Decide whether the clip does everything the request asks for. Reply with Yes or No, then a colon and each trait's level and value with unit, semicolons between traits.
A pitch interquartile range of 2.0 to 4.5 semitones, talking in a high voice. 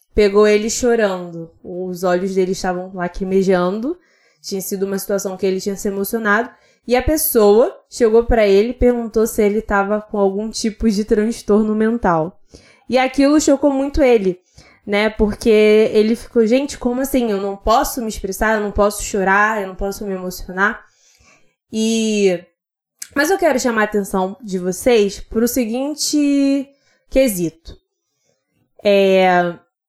Yes: average, 3.7 semitones; high, 215 Hz